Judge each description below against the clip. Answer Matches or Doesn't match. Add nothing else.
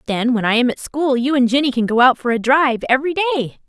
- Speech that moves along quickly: Matches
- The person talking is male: Doesn't match